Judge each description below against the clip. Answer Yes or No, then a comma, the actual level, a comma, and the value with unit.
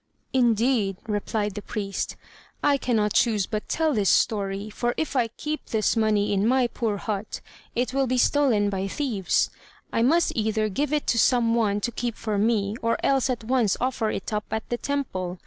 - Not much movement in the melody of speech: No, average, 3.4 semitones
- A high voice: Yes, high, 225 Hz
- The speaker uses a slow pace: No, average, 190 wpm